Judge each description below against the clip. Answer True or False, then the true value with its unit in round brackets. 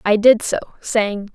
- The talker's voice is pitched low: False (215 Hz)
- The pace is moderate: True (180 wpm)